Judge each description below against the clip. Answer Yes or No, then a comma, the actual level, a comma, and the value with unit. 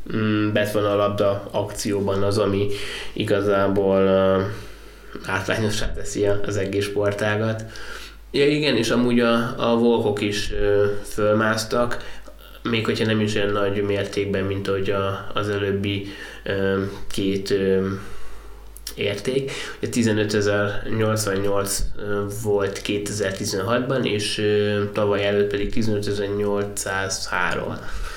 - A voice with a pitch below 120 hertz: Yes, low, 100 Hz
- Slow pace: Yes, slow, 100 wpm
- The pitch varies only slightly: Yes, narrow, 1.0 semitones